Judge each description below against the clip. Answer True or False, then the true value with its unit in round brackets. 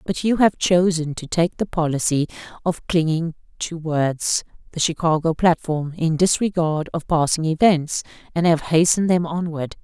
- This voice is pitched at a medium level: True (165 Hz)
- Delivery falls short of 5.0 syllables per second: True (4.3 syllables/s)